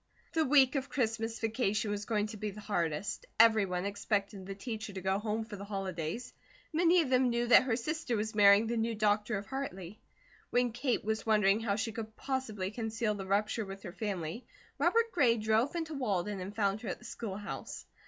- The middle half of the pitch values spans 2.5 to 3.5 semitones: Yes, average, 3.0 semitones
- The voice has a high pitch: Yes, high, 215 Hz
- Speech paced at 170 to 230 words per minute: Yes, average, 200 wpm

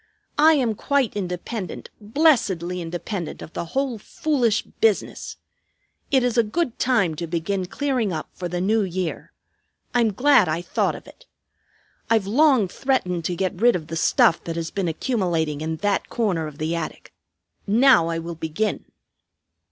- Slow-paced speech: No, average, 160 wpm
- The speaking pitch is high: Yes, high, 195 Hz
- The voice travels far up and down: Yes, wide, 6.3 semitones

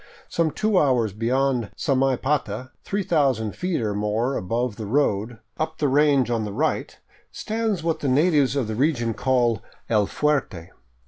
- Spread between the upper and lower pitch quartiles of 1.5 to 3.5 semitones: No, average, 5.0 semitones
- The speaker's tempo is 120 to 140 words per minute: No, average, 155 wpm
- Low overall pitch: Yes, low, 130 Hz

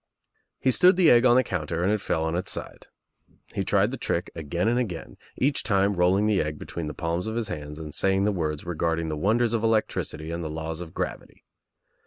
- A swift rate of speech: Yes, fast, 225 wpm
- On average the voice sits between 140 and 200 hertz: No, very low, 90 Hz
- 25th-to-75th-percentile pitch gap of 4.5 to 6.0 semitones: Yes, wide, 5.4 semitones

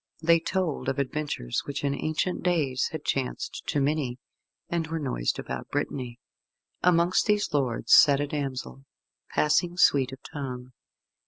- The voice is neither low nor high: Yes, medium, 145 Hz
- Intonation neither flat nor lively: Yes, average, 4.0 semitones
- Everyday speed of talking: Yes, average, 145 wpm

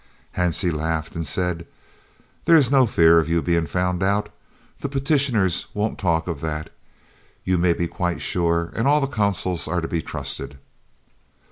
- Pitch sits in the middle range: No, very low, 90 Hz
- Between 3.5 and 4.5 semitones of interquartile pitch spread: Yes, average, 3.9 semitones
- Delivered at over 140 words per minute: Yes, average, 170 wpm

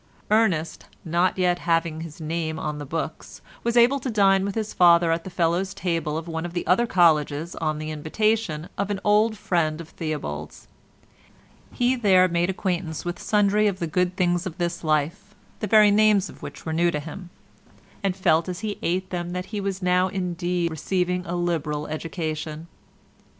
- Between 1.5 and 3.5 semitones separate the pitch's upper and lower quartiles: Yes, average, 3.2 semitones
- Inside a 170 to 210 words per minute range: Yes, average, 185 wpm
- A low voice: No, medium, 175 Hz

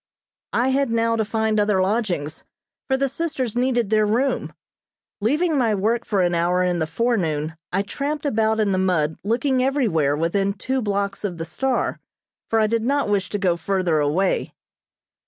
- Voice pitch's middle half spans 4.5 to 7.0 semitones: Yes, average, 5.0 semitones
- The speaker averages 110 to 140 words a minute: No, average, 175 wpm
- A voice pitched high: Yes, high, 210 Hz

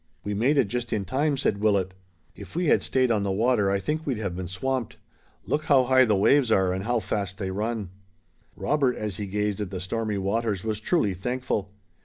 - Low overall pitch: Yes, low, 110 Hz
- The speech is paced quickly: Yes, fast, 215 wpm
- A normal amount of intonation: Yes, average, 4.6 semitones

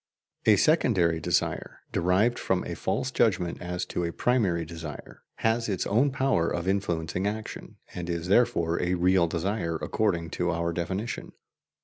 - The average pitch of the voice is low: Yes, very low, 90 Hz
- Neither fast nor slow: Yes, average, 150 wpm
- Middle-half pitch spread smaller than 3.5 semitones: No, average, 4.3 semitones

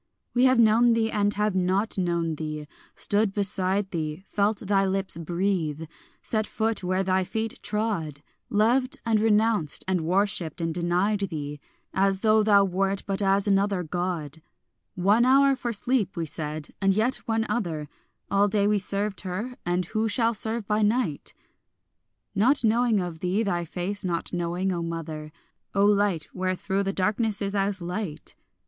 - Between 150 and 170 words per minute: Yes, average, 160 wpm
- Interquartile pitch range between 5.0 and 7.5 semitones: No, average, 3.5 semitones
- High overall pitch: Yes, high, 195 Hz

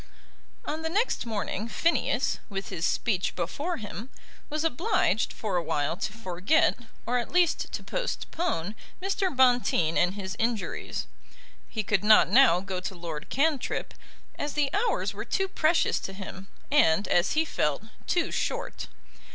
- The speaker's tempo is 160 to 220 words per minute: No, average, 150 wpm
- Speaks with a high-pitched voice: Yes, high, 225 Hz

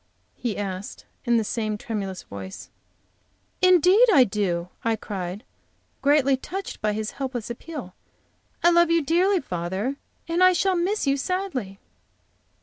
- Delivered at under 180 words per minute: Yes, average, 140 wpm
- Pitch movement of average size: No, wide, 9.0 semitones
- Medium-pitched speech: No, very high, 255 Hz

